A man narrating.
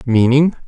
Yes: male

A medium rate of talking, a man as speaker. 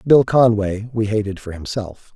Yes: average, 165 wpm; male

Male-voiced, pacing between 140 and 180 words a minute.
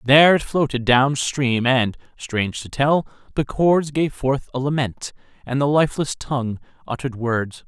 Yes: male; average, 165 wpm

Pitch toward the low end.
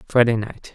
Yes: low, 115 Hz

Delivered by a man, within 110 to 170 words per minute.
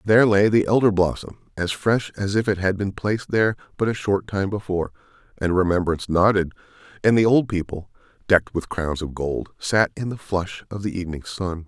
No: male; average, 200 wpm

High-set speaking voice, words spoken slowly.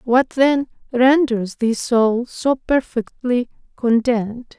Yes: high, 245 Hz; slow, 105 wpm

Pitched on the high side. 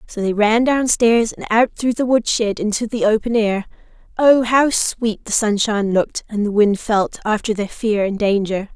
Yes: high, 220 Hz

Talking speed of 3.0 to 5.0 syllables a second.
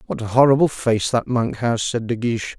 No: 5.4 syllables/s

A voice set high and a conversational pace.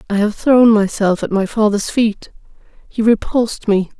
Yes: high, 215 Hz; average, 165 wpm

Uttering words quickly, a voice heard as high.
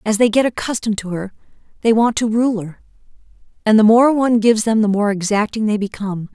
Yes: fast, 210 wpm; high, 220 Hz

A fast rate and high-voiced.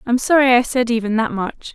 Yes: fast, 240 wpm; high, 240 Hz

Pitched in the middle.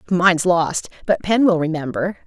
Yes: medium, 170 Hz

